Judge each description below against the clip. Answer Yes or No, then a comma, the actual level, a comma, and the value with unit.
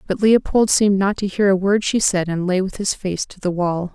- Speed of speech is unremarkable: No, fast, 275 wpm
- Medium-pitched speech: No, high, 195 Hz